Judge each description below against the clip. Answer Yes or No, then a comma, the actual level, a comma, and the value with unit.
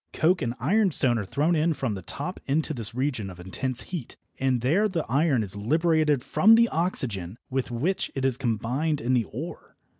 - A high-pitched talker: No, low, 135 Hz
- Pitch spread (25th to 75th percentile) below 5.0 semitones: No, wide, 5.6 semitones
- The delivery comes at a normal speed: Yes, average, 190 wpm